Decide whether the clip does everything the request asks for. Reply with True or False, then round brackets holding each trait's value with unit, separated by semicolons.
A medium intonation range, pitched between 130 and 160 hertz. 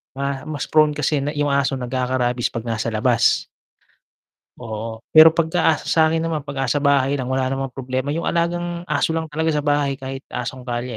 True (3.3 semitones; 140 Hz)